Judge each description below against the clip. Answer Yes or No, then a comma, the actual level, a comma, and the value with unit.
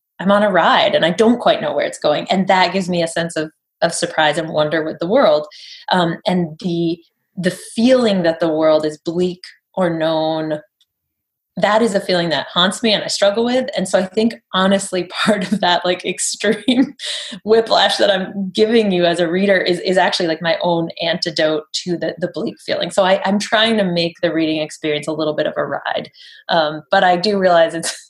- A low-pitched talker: No, medium, 180 Hz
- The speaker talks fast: Yes, fast, 215 wpm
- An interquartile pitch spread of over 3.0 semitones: Yes, average, 3.7 semitones